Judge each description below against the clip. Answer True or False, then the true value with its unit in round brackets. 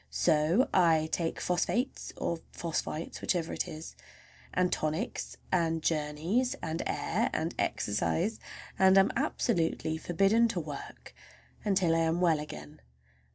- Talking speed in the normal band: False (120 wpm)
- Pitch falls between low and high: True (165 Hz)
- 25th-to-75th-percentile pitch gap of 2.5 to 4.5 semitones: True (3.1 semitones)